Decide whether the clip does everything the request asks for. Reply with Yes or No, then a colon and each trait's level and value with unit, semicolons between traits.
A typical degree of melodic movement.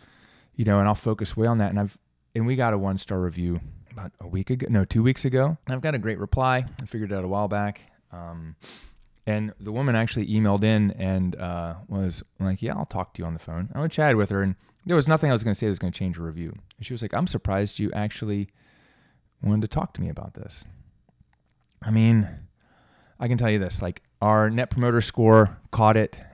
Yes: average, 3.3 semitones